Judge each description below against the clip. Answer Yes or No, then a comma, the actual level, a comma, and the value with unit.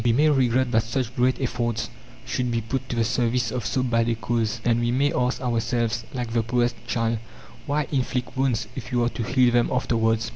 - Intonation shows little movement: Yes, narrow, 1.6 semitones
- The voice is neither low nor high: No, low, 120 Hz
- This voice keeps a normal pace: No, fast, 215 wpm